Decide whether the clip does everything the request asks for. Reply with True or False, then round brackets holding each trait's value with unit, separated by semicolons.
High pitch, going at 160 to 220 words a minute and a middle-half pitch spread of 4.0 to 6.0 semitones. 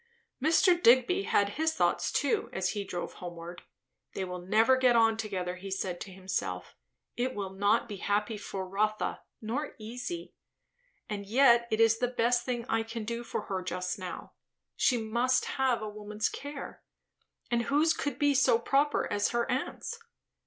True (225 Hz; 170 wpm; 4.4 semitones)